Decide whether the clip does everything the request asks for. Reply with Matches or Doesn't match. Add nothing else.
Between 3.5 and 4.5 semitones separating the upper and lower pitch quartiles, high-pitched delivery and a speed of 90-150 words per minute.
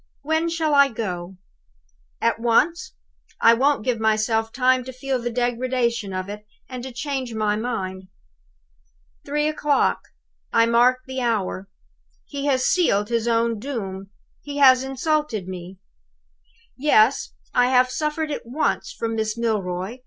Matches